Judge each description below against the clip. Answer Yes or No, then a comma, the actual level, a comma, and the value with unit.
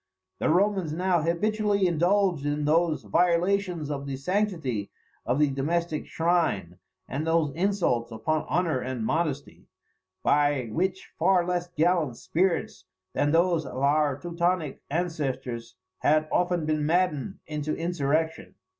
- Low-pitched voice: No, medium, 160 Hz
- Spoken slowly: Yes, slow, 130 wpm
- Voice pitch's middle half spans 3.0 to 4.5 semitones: Yes, average, 3.9 semitones